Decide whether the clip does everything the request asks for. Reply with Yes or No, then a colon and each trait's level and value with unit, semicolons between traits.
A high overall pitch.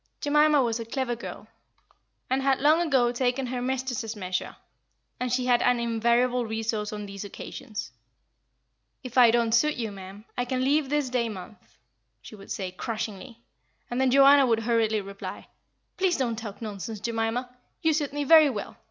Yes: high, 240 Hz